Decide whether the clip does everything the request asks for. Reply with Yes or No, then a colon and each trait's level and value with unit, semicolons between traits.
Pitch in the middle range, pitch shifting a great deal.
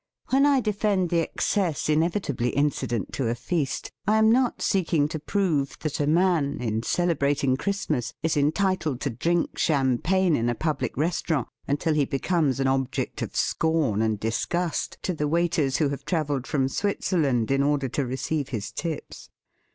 No: medium, 150 Hz; average, 4.5 semitones